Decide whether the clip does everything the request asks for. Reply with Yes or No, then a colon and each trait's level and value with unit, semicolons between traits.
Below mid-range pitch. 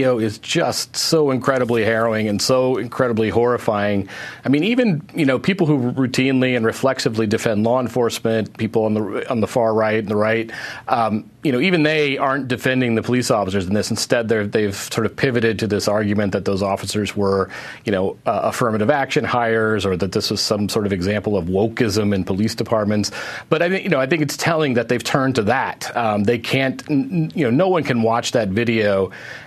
Yes: low, 115 Hz